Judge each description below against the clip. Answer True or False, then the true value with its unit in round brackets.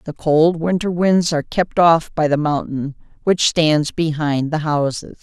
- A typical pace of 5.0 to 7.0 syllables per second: False (4.2 syllables/s)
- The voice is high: False (160 Hz)